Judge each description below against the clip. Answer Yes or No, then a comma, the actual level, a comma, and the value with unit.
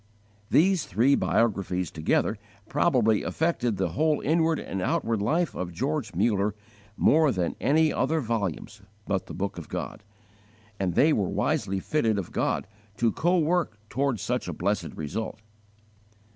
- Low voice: Yes, low, 115 Hz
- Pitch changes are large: Yes, wide, 7.7 semitones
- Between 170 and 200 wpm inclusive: No, average, 145 wpm